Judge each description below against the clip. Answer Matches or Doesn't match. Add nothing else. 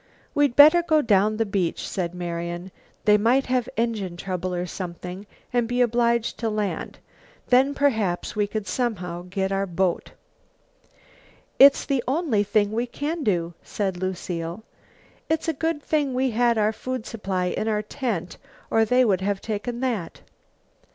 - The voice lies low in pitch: Doesn't match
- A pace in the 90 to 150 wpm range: Doesn't match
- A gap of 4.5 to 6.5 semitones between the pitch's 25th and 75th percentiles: Matches